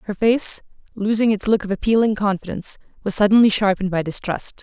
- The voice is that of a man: No, female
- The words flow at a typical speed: Yes, average, 170 wpm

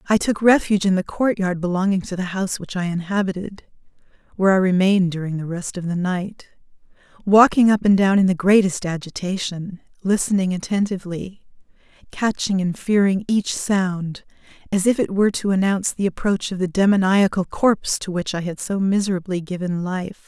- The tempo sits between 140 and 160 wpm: No, average, 170 wpm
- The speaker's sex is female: Yes, female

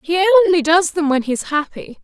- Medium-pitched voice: No, very high, 330 Hz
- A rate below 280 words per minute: Yes, fast, 205 wpm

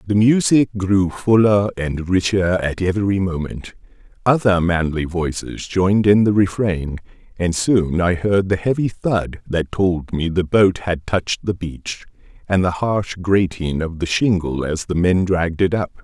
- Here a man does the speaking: Yes, male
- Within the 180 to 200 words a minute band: No, average, 170 wpm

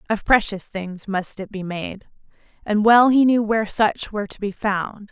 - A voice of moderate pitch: No, high, 210 Hz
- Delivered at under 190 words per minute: No, average, 200 wpm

